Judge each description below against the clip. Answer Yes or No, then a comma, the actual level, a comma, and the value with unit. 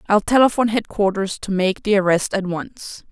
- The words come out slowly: No, average, 175 wpm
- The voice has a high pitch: Yes, high, 200 Hz